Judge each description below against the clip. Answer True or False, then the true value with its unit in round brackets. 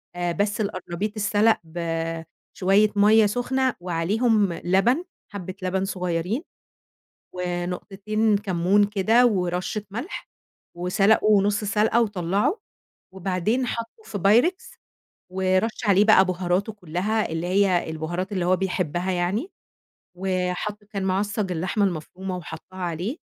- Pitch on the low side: False (195 Hz)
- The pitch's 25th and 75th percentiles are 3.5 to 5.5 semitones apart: False (3.0 semitones)